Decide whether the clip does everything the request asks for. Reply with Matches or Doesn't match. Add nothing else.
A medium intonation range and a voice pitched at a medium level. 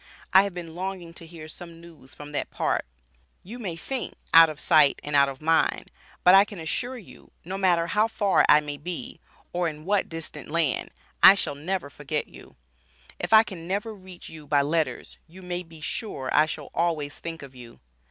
Matches